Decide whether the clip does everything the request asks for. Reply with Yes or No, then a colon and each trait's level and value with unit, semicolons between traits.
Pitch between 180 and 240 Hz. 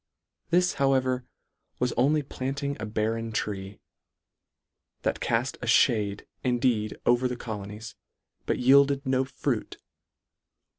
No: low, 125 Hz